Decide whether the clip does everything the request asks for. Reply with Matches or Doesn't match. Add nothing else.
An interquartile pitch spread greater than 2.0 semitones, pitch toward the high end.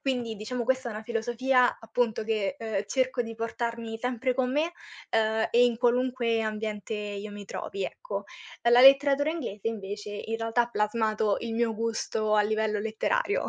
Matches